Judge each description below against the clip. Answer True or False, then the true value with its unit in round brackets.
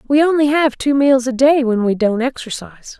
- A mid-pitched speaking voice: False (260 Hz)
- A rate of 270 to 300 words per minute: False (220 wpm)